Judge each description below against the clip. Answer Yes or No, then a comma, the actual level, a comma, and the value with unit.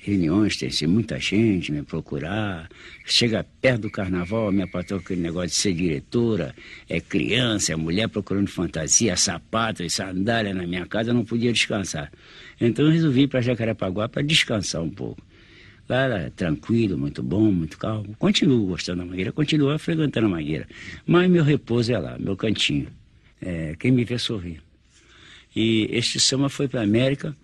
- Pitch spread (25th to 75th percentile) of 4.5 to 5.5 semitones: Yes, average, 5.1 semitones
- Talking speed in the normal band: Yes, average, 175 wpm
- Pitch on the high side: No, low, 110 Hz